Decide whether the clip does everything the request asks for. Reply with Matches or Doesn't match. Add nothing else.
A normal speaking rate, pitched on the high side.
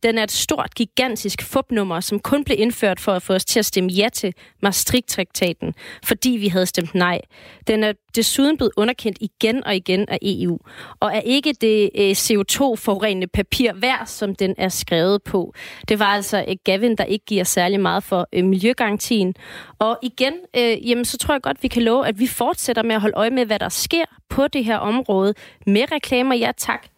Matches